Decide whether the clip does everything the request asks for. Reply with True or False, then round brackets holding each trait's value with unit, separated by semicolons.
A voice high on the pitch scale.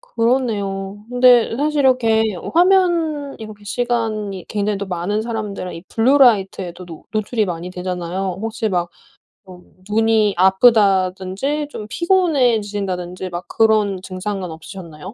True (210 Hz)